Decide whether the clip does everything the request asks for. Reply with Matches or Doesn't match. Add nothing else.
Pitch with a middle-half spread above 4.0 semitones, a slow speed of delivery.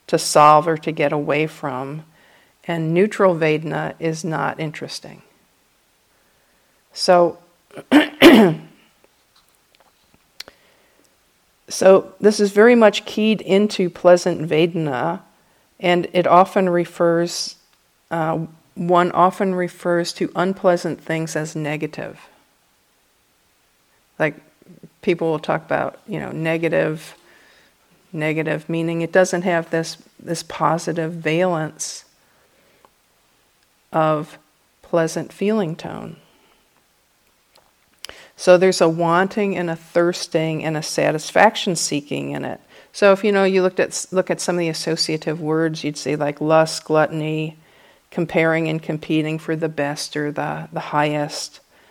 Doesn't match